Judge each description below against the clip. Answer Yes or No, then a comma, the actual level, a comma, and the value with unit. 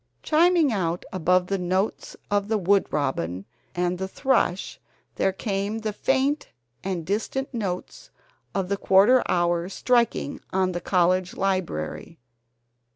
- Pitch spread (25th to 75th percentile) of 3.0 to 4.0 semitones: Yes, average, 3.5 semitones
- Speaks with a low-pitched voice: No, high, 190 Hz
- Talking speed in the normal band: No, slow, 130 wpm